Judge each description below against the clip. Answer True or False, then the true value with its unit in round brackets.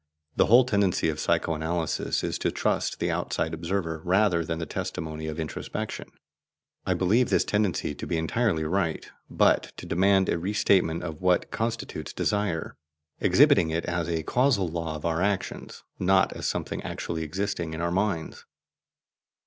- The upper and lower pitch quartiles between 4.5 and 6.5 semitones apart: False (3.4 semitones)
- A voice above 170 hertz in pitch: False (85 Hz)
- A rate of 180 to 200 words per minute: False (165 wpm)